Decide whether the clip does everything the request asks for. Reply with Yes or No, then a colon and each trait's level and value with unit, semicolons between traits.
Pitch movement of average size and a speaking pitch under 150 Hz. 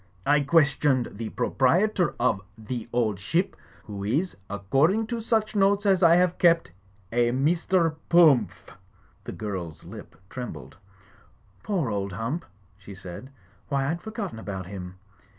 No: wide, 8.7 semitones; medium, 140 Hz